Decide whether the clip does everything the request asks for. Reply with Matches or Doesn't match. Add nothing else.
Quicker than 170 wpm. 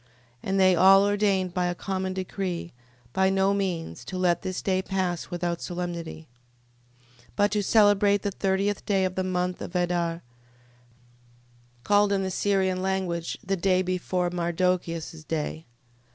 Doesn't match